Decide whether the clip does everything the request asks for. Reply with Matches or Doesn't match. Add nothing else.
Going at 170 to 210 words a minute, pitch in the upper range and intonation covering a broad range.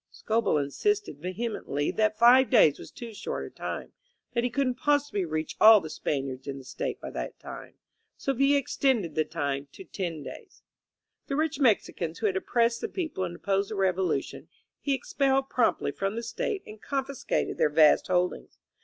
Matches